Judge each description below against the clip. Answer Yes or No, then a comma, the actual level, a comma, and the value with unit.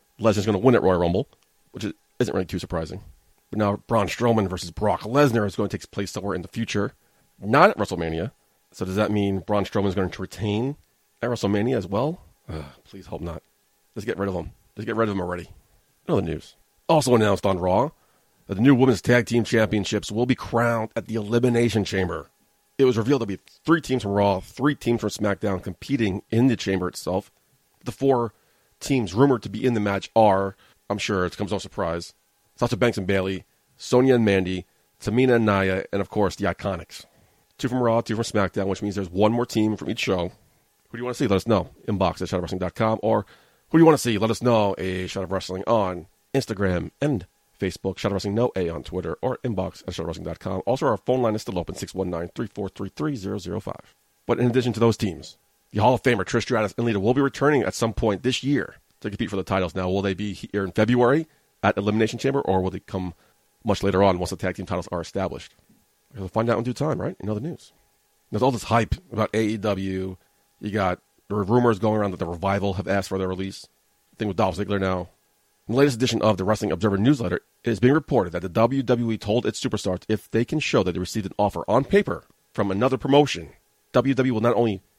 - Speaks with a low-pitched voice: Yes, low, 105 Hz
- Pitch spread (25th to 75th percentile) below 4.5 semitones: Yes, average, 3.7 semitones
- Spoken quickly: Yes, fast, 230 wpm